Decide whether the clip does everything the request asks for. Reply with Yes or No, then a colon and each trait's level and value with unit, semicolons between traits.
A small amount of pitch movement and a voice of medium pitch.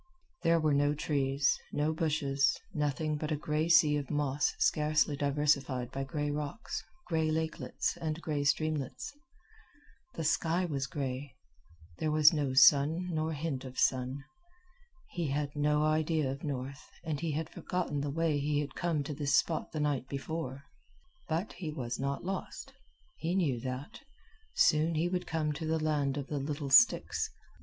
Yes: narrow, 2.3 semitones; medium, 150 Hz